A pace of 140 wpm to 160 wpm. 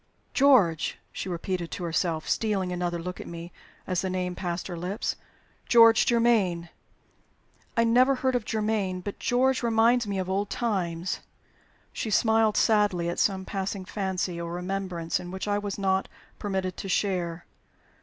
Yes: average, 155 wpm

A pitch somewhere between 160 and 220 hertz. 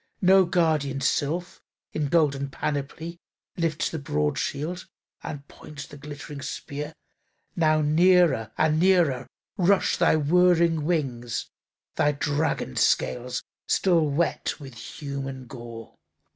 No: medium, 150 Hz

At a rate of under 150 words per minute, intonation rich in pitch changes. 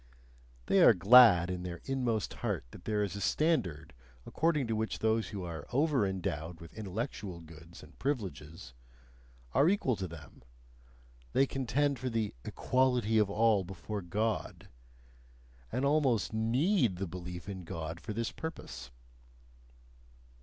Yes: average, 140 wpm; wide, 6.2 semitones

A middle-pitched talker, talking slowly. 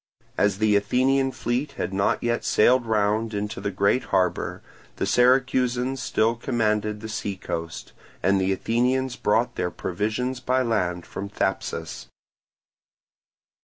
No: low, 110 Hz; slow, 130 wpm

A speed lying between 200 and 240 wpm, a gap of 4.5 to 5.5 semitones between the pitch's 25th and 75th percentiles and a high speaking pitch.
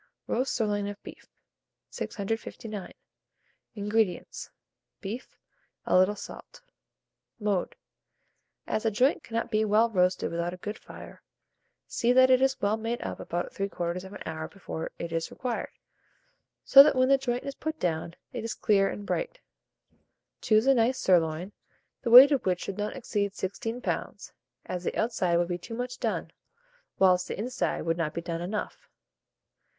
No: average, 155 wpm; average, 4.9 semitones; high, 210 Hz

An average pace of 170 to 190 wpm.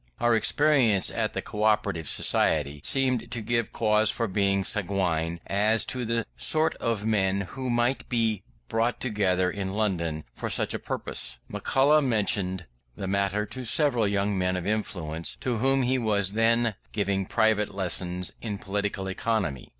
No: average, 160 wpm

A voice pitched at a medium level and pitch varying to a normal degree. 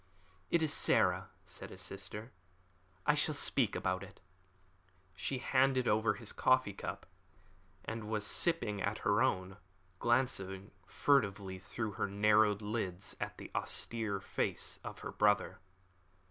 No: low, 105 Hz; average, 3.4 semitones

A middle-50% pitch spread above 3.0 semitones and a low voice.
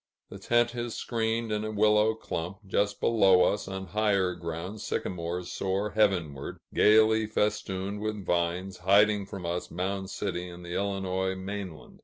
No: average, 2.7 semitones; low, 100 Hz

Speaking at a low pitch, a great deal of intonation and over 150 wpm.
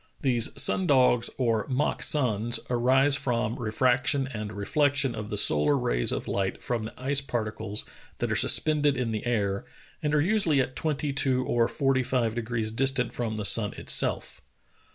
No: low, 125 Hz; average, 3.7 semitones; average, 175 wpm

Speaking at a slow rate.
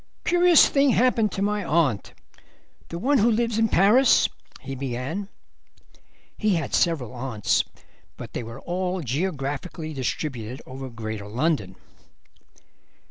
Yes: slow, 125 wpm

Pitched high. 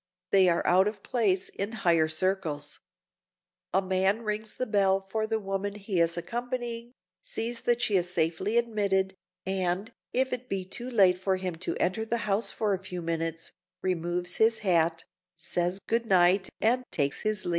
Yes: high, 195 Hz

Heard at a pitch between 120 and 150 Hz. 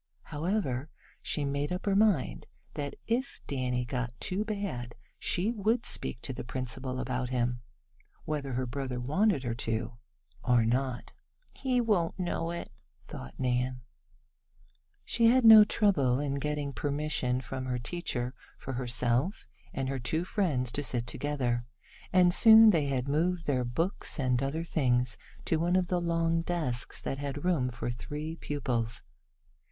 Yes: medium, 140 Hz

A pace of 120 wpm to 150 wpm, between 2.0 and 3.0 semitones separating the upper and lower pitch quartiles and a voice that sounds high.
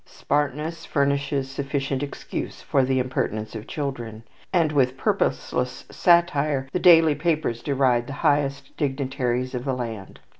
No: slow, 135 wpm; narrow, 2.6 semitones; low, 135 Hz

